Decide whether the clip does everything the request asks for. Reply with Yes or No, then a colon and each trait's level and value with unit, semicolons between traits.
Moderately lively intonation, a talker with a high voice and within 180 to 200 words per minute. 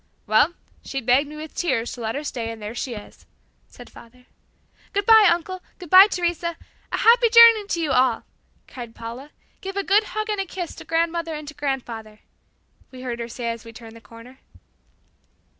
No: wide, 7.5 semitones; very high, 285 Hz; average, 195 wpm